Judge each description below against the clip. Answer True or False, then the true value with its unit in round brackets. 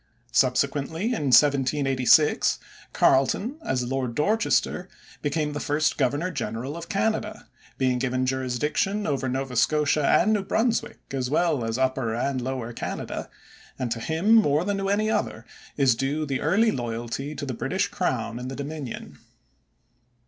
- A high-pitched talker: False (140 Hz)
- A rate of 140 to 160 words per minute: True (150 wpm)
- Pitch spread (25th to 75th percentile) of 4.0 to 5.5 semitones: True (4.5 semitones)